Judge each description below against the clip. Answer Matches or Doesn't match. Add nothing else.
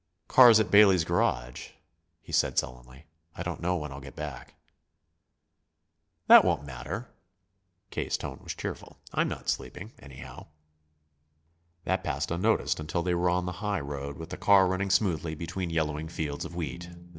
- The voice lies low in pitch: Matches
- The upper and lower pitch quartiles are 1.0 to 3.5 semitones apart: Doesn't match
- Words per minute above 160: Doesn't match